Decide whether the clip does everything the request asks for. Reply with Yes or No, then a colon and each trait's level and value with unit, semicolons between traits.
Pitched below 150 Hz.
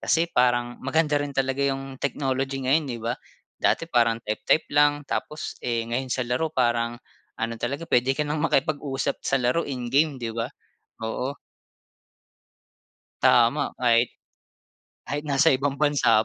Yes: low, 135 Hz